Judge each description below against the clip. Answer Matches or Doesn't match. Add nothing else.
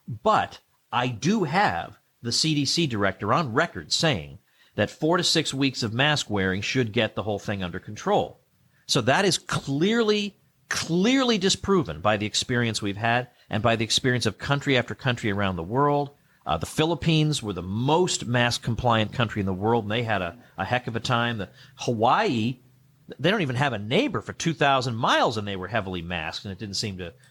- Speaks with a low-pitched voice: Matches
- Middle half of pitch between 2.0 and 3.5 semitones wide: Doesn't match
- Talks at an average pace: Matches